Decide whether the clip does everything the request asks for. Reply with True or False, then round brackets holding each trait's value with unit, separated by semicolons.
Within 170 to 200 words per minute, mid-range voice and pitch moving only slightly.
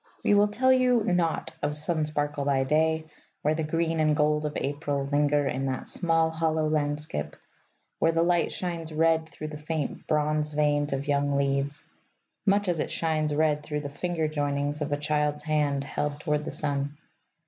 True (180 wpm; 150 Hz; 1.8 semitones)